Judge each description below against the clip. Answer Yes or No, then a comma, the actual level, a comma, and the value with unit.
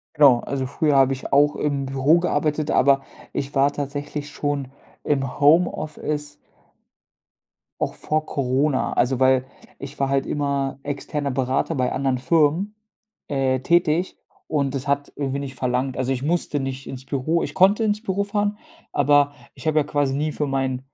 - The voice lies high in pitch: No, medium, 140 Hz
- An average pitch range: No, narrow, 2.2 semitones